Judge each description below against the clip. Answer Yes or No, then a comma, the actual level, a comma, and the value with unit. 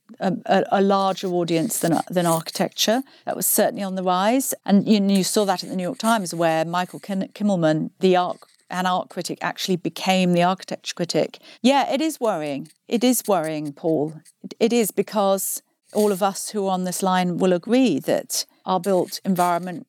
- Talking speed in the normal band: Yes, average, 190 wpm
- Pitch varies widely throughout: No, average, 3.3 semitones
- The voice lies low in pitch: No, high, 190 Hz